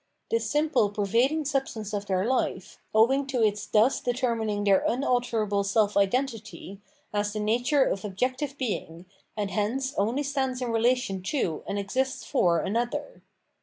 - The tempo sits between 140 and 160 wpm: Yes, average, 150 wpm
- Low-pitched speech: No, high, 225 Hz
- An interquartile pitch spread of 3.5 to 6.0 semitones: Yes, average, 4.2 semitones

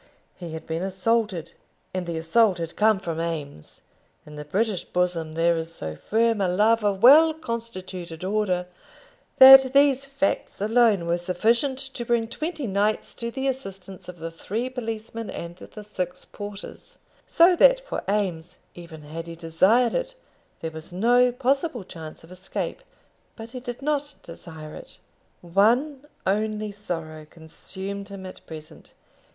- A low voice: No, high, 200 Hz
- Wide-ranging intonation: Yes, wide, 5.9 semitones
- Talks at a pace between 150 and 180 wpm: Yes, average, 155 wpm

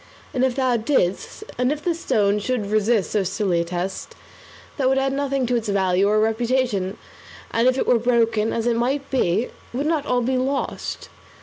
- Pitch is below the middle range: No, high, 235 Hz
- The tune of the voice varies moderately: Yes, average, 4.1 semitones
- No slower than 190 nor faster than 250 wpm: Yes, average, 195 wpm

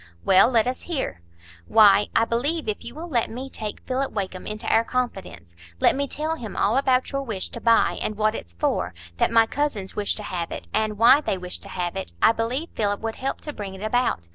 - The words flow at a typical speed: No, fast, 220 wpm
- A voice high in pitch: Yes, high, 225 Hz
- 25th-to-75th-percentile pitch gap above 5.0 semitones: No, average, 4.7 semitones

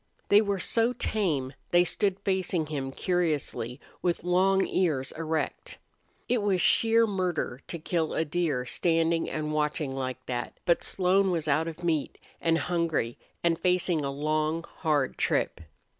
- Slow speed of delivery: No, average, 150 wpm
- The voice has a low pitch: No, medium, 165 Hz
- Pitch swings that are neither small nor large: Yes, average, 3.4 semitones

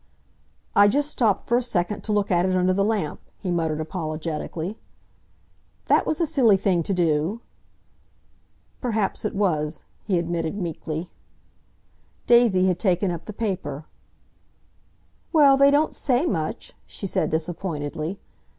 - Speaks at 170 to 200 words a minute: No, average, 140 wpm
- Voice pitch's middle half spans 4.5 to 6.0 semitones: Yes, average, 4.9 semitones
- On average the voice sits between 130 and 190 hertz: Yes, medium, 185 Hz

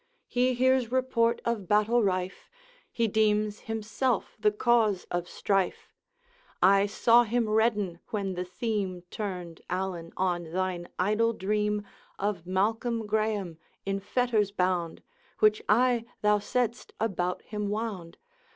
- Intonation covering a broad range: No, average, 3.4 semitones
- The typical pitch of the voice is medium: No, high, 210 Hz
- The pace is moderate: No, slow, 125 wpm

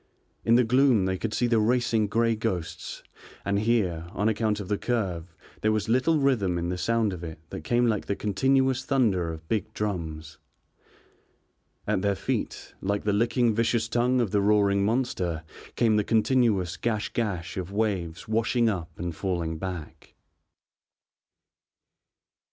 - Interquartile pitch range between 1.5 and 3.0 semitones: No, average, 4.3 semitones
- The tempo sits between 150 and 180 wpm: Yes, average, 155 wpm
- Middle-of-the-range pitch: No, low, 105 Hz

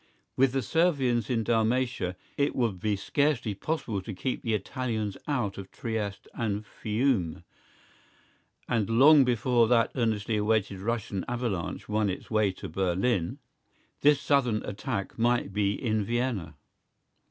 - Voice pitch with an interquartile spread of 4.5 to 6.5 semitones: No, average, 3.6 semitones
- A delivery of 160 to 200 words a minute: No, slow, 135 wpm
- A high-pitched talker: No, low, 110 Hz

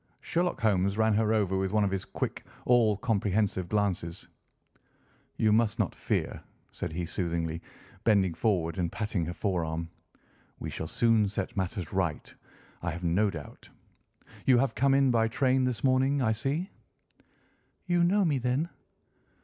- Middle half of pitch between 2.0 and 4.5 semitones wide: No, wide, 5.4 semitones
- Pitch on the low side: Yes, low, 105 Hz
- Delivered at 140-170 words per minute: Yes, average, 155 wpm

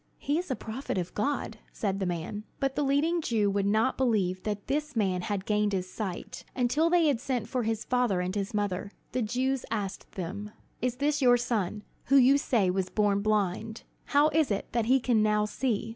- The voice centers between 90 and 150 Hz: No, high, 220 Hz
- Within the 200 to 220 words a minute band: Yes, fast, 205 wpm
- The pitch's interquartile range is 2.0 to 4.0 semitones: No, average, 4.6 semitones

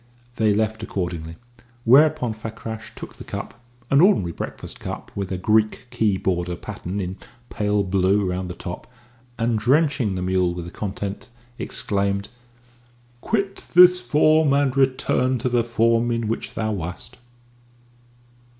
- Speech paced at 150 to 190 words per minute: No, average, 140 wpm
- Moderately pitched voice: No, low, 110 Hz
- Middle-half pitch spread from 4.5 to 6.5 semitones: Yes, average, 4.9 semitones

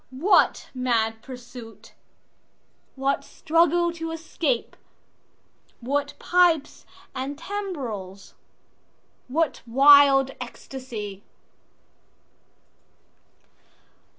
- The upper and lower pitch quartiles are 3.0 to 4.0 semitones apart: No, average, 5.2 semitones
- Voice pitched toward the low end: No, very high, 270 Hz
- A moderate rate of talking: No, slow, 55 wpm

